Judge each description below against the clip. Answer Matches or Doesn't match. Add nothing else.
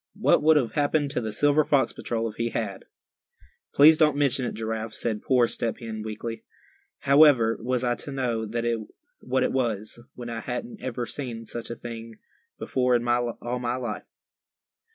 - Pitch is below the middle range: Matches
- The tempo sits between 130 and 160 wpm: Doesn't match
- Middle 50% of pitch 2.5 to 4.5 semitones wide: Matches